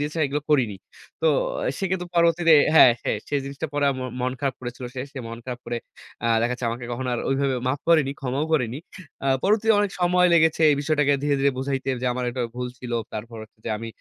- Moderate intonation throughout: Yes, average, 4.1 semitones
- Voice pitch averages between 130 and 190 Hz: Yes, low, 135 Hz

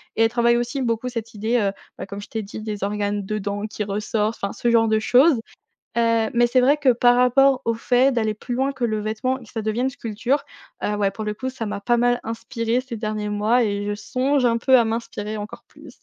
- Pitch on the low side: No, high, 230 Hz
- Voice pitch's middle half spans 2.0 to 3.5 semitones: Yes, average, 2.7 semitones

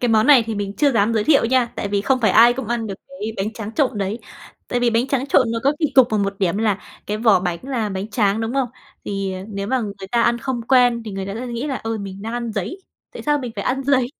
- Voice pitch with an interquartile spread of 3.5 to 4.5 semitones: Yes, average, 3.8 semitones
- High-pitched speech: Yes, high, 230 Hz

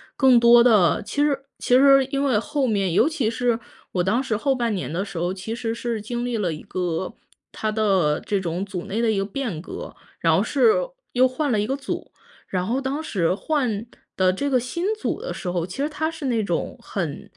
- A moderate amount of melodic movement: No, wide, 5.8 semitones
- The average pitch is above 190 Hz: Yes, high, 230 Hz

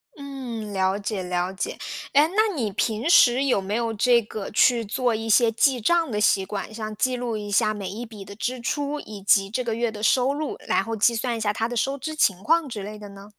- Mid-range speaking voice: No, high, 225 Hz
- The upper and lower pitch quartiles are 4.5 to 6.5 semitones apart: No, average, 3.7 semitones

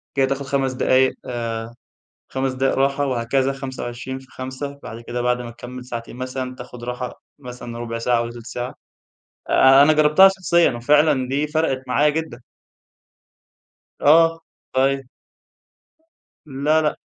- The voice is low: Yes, low, 130 Hz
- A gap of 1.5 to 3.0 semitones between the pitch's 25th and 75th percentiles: Yes, narrow, 2.4 semitones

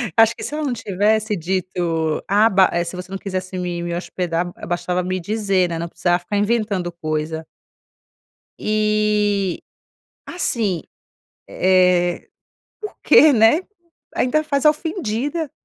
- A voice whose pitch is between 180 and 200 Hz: Yes, high, 190 Hz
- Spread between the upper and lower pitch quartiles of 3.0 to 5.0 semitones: Yes, average, 3.9 semitones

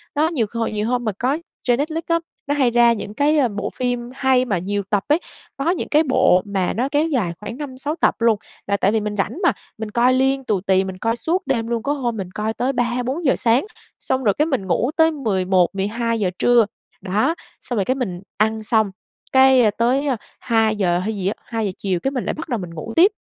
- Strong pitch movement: No, average, 4.5 semitones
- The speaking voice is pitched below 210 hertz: No, high, 235 Hz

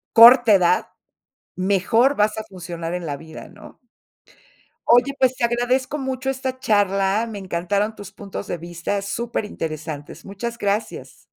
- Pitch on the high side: Yes, high, 205 Hz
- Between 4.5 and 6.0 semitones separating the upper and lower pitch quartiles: Yes, average, 5.0 semitones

